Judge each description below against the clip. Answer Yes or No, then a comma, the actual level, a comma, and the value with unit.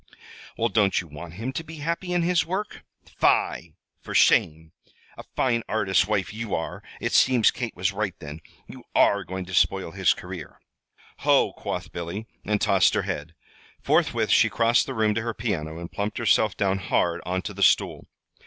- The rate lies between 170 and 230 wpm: Yes, average, 185 wpm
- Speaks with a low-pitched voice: Yes, low, 100 Hz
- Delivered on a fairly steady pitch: No, average, 4.4 semitones